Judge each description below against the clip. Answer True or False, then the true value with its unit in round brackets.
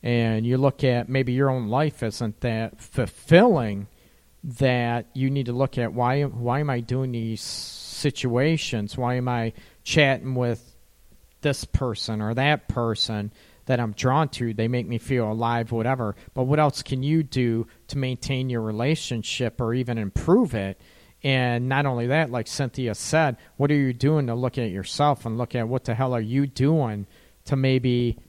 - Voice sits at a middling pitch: False (125 Hz)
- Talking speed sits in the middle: True (180 wpm)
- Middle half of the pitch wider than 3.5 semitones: False (3.0 semitones)